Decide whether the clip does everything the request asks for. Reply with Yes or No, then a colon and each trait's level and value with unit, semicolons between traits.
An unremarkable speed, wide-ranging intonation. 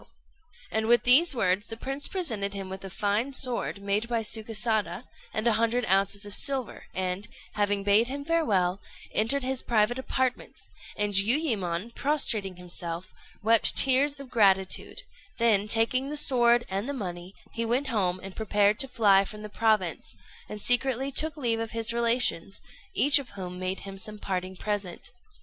No: average, 170 wpm; average, 4.1 semitones